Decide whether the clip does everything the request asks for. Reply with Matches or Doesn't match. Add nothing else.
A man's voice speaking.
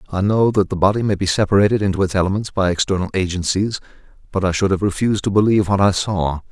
Matches